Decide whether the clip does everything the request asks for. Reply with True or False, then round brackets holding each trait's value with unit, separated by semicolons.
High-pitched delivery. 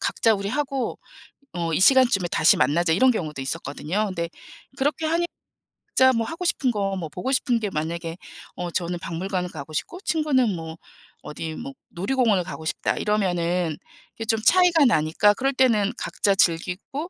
True (195 Hz)